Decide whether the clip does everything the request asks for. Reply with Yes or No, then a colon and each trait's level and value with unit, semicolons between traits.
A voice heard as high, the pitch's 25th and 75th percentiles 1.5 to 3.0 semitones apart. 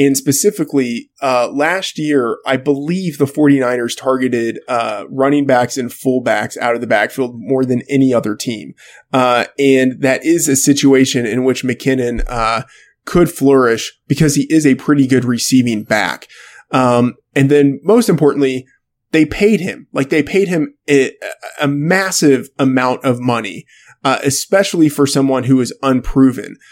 No: low, 135 Hz; narrow, 2.4 semitones